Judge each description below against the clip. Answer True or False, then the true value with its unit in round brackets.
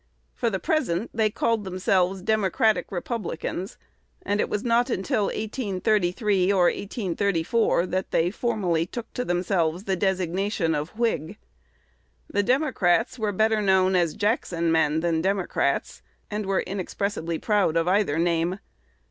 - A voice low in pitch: False (190 Hz)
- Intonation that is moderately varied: True (3.6 semitones)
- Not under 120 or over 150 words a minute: True (140 wpm)